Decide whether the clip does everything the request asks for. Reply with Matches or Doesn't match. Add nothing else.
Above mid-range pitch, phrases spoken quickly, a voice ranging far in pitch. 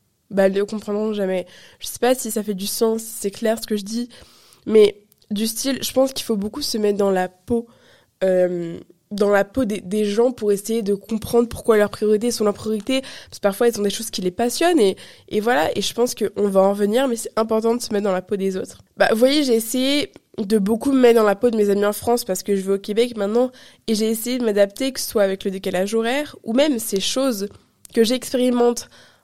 Doesn't match